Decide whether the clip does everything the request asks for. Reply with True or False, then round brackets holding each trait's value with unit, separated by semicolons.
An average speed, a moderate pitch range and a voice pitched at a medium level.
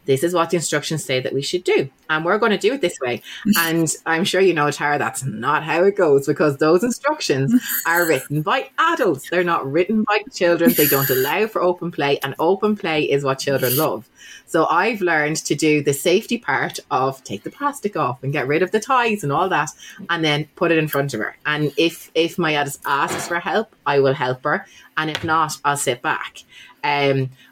False (225 wpm; 4.2 semitones; 160 Hz)